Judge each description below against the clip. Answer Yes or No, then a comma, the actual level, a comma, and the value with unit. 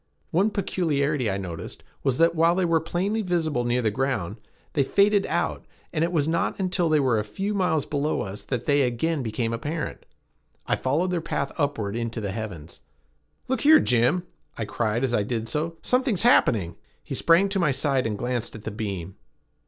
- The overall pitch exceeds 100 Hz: Yes, medium, 140 Hz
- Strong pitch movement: Yes, wide, 6.9 semitones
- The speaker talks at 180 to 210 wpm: Yes, average, 190 wpm